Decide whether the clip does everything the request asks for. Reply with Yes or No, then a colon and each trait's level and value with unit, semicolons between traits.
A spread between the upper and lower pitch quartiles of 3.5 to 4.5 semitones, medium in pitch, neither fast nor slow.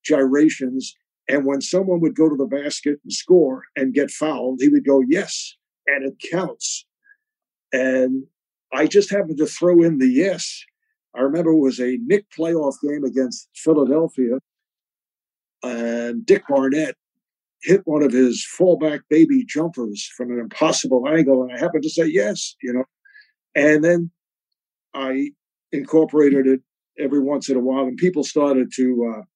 Yes: average, 4.2 semitones; medium, 145 Hz; average, 155 wpm